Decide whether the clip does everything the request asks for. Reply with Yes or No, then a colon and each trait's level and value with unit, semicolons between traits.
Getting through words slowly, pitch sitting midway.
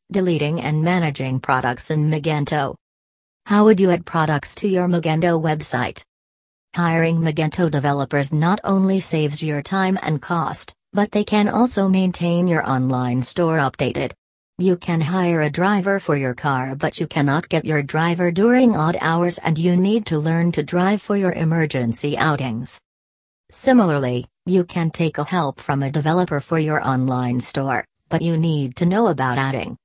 No: average, 165 wpm; medium, 160 Hz